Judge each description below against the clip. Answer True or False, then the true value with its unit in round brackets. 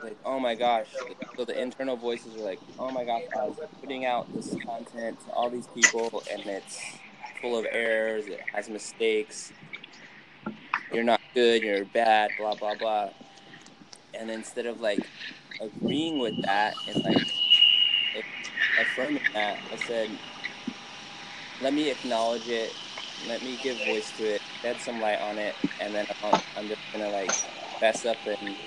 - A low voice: True (115 Hz)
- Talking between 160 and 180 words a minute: True (165 wpm)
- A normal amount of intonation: False (2.3 semitones)